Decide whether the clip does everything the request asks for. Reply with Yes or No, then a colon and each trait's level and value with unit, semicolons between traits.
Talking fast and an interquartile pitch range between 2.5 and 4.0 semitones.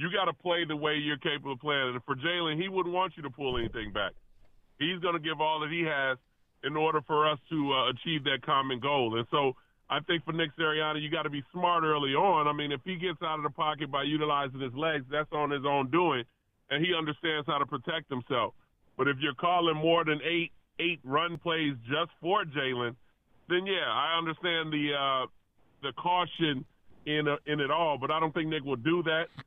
Yes: fast, 230 wpm; average, 2.8 semitones